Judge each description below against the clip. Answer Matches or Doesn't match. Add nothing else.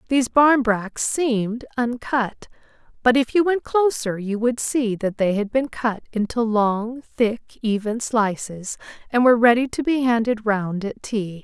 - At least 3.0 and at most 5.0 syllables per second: Matches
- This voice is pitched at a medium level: Doesn't match